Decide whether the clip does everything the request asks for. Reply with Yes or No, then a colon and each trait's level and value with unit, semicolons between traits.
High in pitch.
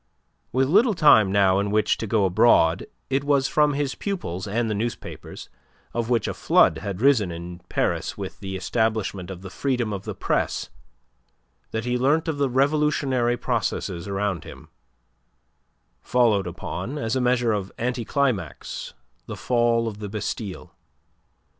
No: low, 115 Hz